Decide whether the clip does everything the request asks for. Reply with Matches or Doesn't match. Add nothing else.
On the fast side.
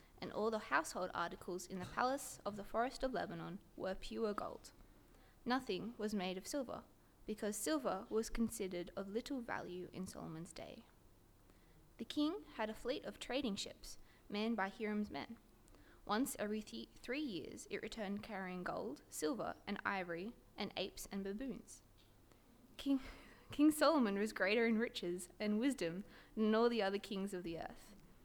Doesn't match